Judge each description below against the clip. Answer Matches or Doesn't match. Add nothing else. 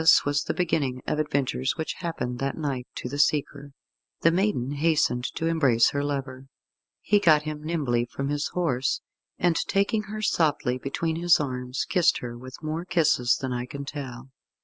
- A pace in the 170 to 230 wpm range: Matches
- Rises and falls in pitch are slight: Doesn't match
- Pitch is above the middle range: Doesn't match